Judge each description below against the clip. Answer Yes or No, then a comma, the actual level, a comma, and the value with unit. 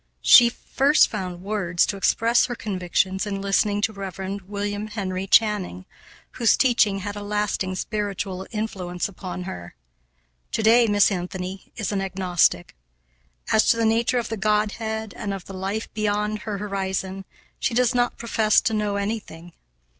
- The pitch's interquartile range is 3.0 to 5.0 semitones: No, narrow, 2.4 semitones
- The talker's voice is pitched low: No, high, 205 Hz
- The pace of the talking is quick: No, average, 155 wpm